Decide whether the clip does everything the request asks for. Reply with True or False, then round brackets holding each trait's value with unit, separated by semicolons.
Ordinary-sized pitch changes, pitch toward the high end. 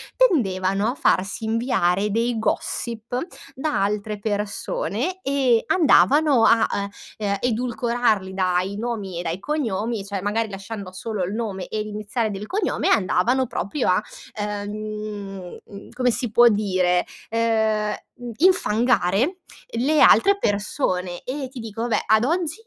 True (3.5 semitones; 215 Hz)